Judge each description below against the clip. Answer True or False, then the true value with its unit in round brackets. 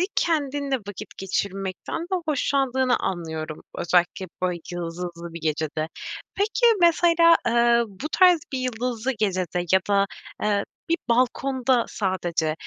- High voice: True (210 Hz)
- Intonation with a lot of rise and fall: True (7.3 semitones)